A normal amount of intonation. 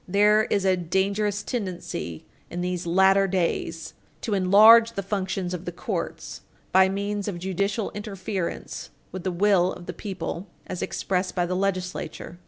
No: narrow, 2.1 semitones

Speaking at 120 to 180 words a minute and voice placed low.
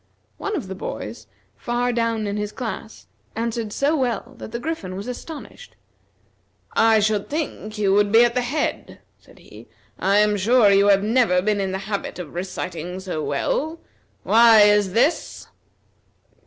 No: average, 165 wpm; high, 210 Hz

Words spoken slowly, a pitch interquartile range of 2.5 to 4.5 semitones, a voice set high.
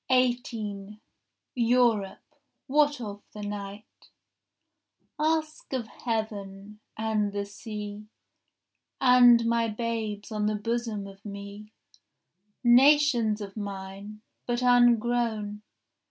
Yes: slow, 95 wpm; average, 2.8 semitones; high, 220 Hz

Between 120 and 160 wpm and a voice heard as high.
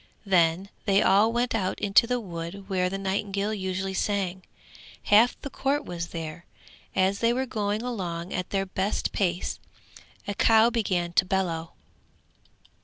Yes: average, 150 wpm; high, 195 Hz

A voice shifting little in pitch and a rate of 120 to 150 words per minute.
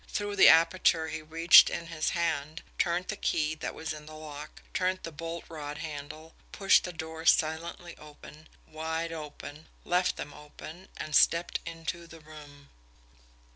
No: narrow, 1.7 semitones; average, 160 wpm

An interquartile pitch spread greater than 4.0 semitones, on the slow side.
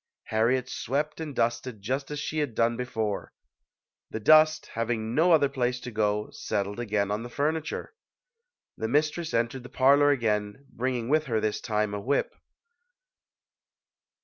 No: average, 4.6 semitones; average, 160 wpm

